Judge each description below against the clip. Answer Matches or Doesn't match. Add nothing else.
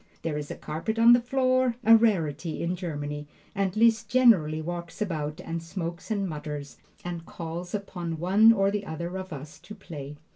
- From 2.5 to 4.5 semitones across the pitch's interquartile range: Doesn't match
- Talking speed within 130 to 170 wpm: Doesn't match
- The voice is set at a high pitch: Doesn't match